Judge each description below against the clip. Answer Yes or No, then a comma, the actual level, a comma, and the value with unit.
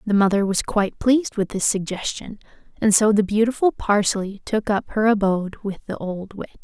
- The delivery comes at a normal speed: Yes, average, 190 wpm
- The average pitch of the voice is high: Yes, high, 205 Hz